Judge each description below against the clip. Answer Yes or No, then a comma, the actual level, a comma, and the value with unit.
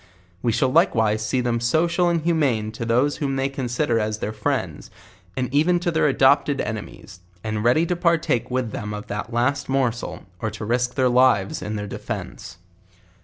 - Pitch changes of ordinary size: Yes, average, 4.8 semitones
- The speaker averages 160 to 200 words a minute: Yes, average, 190 wpm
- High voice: No, low, 125 Hz